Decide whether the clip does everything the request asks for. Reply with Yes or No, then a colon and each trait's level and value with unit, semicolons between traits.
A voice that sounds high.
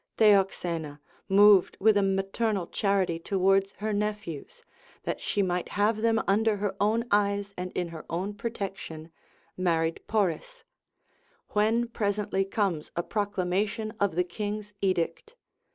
Yes: high, 200 Hz